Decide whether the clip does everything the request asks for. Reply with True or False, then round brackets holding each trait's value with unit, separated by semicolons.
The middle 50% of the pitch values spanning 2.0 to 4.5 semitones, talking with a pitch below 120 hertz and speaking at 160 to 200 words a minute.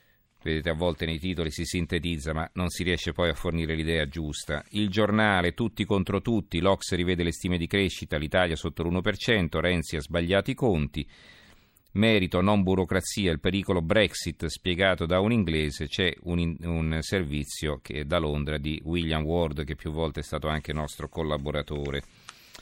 True (3.5 semitones; 85 Hz; 170 wpm)